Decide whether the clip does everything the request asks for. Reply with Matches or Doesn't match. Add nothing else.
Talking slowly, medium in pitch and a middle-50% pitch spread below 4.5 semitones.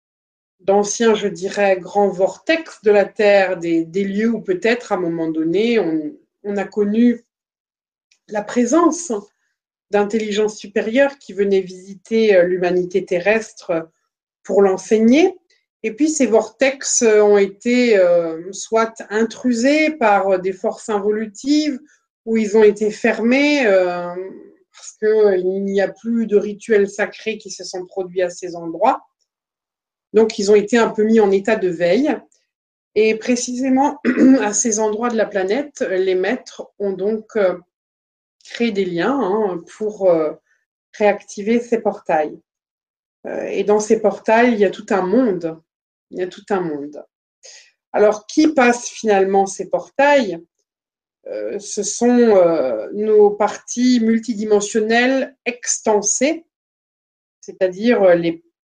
Doesn't match